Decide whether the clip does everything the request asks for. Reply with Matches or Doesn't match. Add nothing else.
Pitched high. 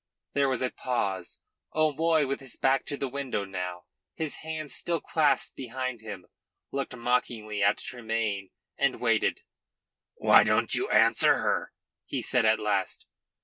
Doesn't match